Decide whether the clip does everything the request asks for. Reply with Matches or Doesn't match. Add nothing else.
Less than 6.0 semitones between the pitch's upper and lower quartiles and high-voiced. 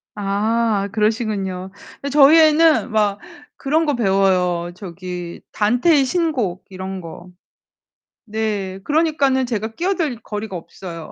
Doesn't match